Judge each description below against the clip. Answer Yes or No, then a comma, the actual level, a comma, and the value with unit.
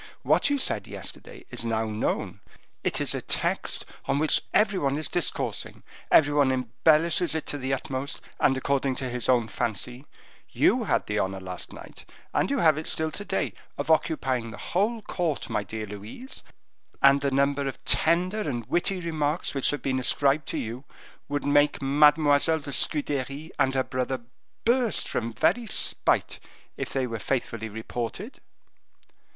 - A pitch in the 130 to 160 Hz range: Yes, medium, 140 Hz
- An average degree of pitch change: Yes, average, 4.1 semitones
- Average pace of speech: Yes, average, 170 wpm